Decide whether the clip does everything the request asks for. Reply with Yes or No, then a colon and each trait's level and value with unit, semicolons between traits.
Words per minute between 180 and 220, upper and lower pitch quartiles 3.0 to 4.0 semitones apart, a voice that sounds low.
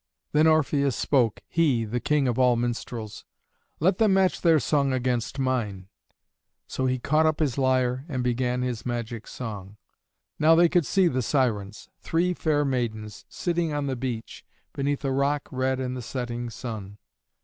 No: average, 165 wpm; average, 3.7 semitones; low, 130 Hz